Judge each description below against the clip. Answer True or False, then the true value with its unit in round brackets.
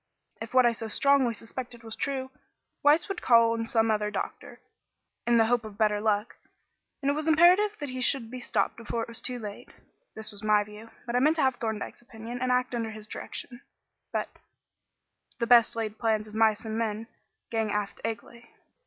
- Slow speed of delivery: False (200 wpm)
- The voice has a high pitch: True (230 Hz)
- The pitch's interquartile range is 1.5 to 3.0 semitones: True (2.5 semitones)